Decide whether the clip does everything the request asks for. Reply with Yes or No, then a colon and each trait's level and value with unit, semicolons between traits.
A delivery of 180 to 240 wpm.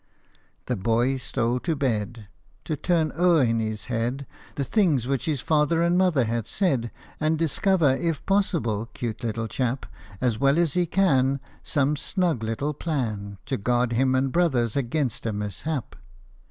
No: average, 160 wpm